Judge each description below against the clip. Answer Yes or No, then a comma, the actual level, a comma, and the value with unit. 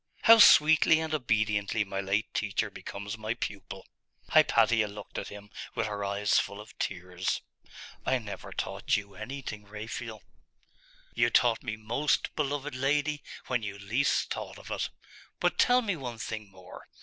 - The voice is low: Yes, low, 110 Hz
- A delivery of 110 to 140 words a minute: No, average, 155 wpm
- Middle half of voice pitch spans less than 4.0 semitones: No, average, 4.7 semitones